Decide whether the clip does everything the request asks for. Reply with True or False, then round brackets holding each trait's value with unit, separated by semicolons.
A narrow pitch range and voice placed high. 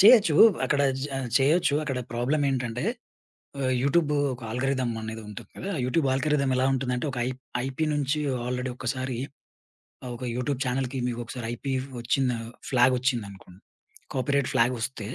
False (2.3 semitones; 130 Hz)